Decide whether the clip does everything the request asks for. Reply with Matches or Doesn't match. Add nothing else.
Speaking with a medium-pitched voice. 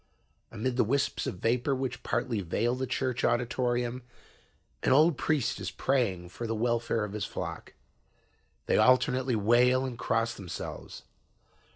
Doesn't match